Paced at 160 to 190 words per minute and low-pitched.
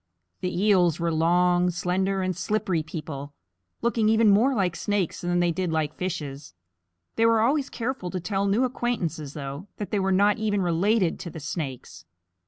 No: average, 175 wpm; medium, 185 Hz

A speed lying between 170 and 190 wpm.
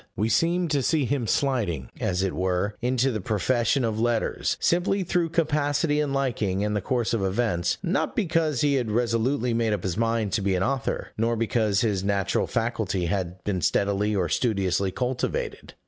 Yes: average, 180 wpm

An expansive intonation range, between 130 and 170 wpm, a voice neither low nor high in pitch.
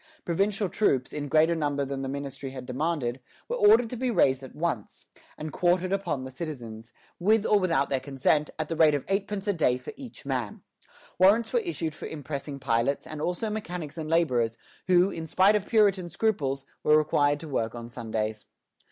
No: wide, 6.0 semitones; average, 190 wpm; medium, 155 Hz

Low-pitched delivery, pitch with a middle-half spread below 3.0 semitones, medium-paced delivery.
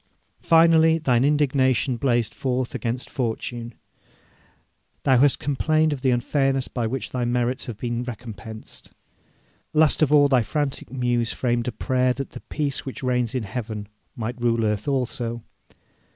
Yes: low, 125 Hz; narrow, 2.5 semitones; average, 150 wpm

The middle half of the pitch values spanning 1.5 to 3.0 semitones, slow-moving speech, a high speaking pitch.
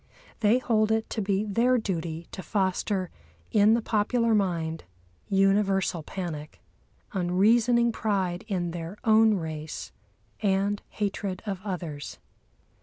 No: average, 3.5 semitones; slow, 115 wpm; high, 195 Hz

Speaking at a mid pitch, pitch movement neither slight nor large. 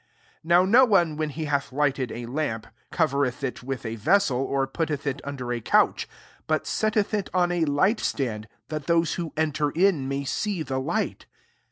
Yes: medium, 150 Hz; average, 4.3 semitones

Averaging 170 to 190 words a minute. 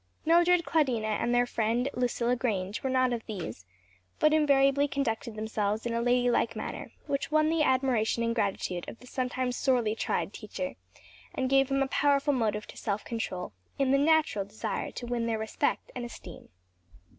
Yes: average, 175 wpm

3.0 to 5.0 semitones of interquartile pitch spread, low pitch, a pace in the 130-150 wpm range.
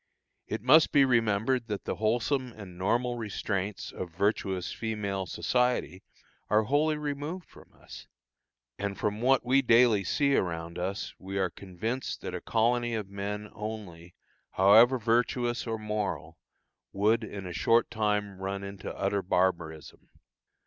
Yes: average, 3.7 semitones; low, 105 Hz; average, 140 wpm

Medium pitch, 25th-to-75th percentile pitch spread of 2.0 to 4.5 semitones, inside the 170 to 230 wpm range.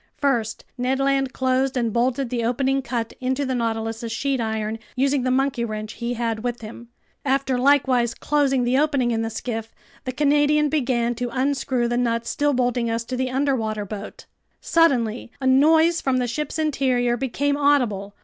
No: very high, 255 Hz; average, 2.8 semitones; average, 175 wpm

